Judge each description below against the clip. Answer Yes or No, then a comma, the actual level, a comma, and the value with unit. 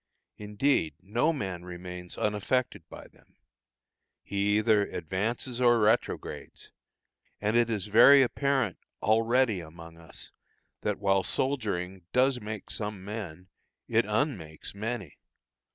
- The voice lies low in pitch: Yes, low, 105 Hz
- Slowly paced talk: Yes, slow, 120 wpm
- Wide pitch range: No, average, 4.3 semitones